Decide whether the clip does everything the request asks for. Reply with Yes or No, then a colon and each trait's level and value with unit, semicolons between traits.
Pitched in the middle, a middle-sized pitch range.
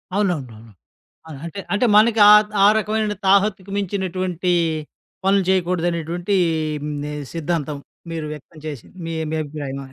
Yes: medium, 175 Hz; average, 4.8 semitones